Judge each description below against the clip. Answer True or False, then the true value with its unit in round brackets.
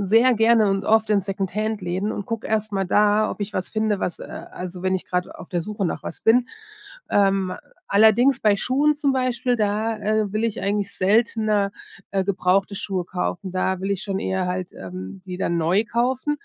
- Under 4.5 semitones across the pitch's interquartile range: True (2.7 semitones)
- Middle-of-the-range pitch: False (205 Hz)